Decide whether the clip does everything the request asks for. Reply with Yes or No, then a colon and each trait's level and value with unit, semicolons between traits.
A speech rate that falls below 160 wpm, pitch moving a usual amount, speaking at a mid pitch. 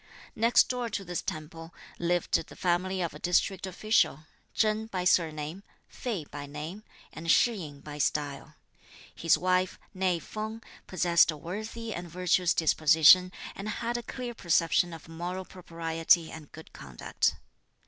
Yes: average, 150 wpm; average, 3.2 semitones; medium, 175 Hz